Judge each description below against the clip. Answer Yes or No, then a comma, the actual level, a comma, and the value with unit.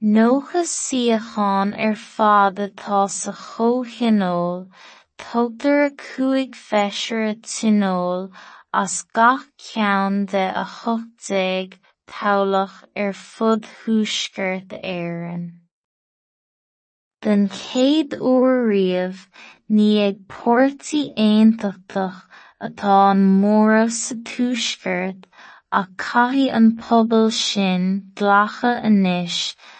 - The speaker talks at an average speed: No, slow, 95 wpm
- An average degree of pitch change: Yes, average, 3.2 semitones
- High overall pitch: Yes, high, 210 Hz